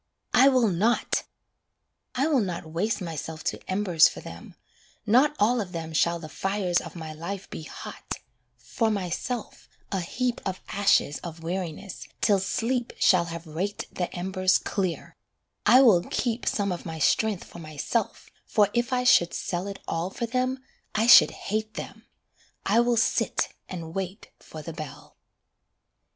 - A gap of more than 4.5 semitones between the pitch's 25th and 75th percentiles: Yes, average, 5.0 semitones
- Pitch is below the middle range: No, high, 190 Hz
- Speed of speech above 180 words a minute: No, average, 160 wpm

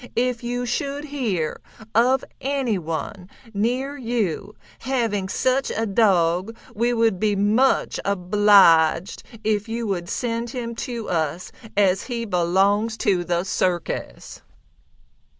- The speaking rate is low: Yes, slow, 115 wpm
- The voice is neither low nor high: No, high, 215 Hz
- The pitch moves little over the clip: No, average, 4.6 semitones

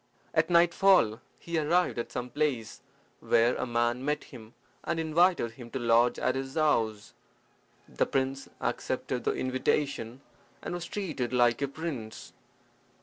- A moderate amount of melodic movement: Yes, average, 5.0 semitones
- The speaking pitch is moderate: No, low, 130 Hz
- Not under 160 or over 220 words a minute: No, average, 145 wpm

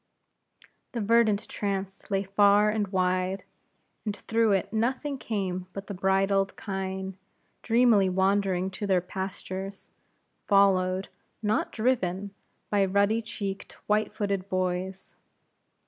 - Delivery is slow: Yes, slow, 115 wpm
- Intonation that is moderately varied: No, narrow, 1.7 semitones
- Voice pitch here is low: No, high, 195 Hz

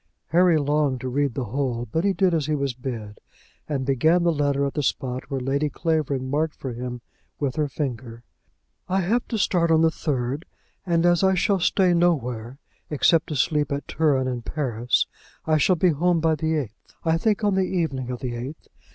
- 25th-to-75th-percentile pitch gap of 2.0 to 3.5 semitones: No, average, 4.3 semitones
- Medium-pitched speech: Yes, medium, 145 Hz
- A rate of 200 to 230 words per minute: Yes, fast, 205 wpm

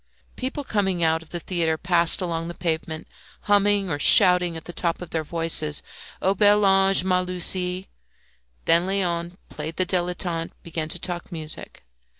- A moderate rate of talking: Yes, average, 160 wpm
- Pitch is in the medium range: Yes, medium, 175 Hz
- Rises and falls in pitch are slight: Yes, narrow, 2.3 semitones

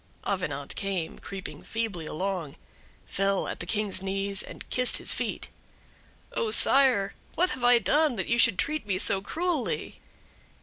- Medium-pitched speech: No, high, 200 Hz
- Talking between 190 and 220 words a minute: No, average, 150 wpm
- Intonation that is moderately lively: Yes, average, 4.8 semitones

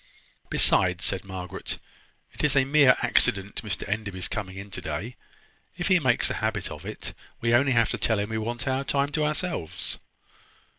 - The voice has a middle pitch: No, low, 115 Hz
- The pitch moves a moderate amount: No, wide, 6.1 semitones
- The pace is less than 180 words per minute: No, average, 190 wpm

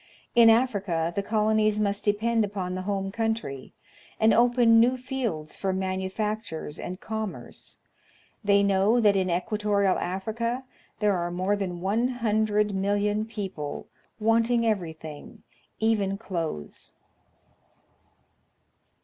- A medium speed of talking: No, slow, 110 wpm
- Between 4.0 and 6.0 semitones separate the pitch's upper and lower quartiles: No, average, 2.9 semitones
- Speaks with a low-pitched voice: No, high, 205 Hz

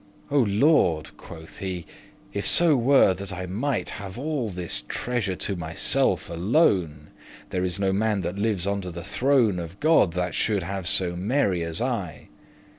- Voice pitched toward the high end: No, very low, 95 Hz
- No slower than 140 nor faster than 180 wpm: Yes, average, 165 wpm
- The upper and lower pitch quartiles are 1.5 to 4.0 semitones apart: No, average, 4.8 semitones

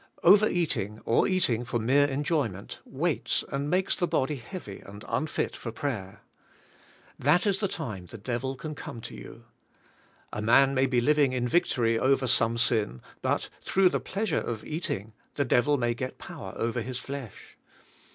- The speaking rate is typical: Yes, average, 165 wpm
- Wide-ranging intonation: No, average, 4.7 semitones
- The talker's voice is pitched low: Yes, low, 130 Hz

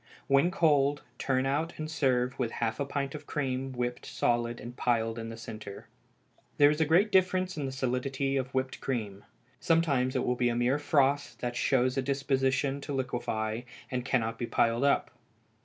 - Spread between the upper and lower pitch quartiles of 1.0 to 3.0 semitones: Yes, average, 2.7 semitones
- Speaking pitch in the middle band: No, low, 130 Hz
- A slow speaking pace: No, average, 185 wpm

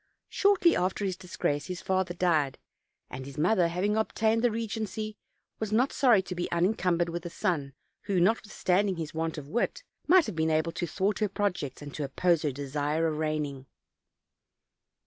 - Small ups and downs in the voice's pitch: No, average, 5.3 semitones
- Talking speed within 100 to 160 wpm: No, average, 185 wpm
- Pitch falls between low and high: Yes, medium, 180 Hz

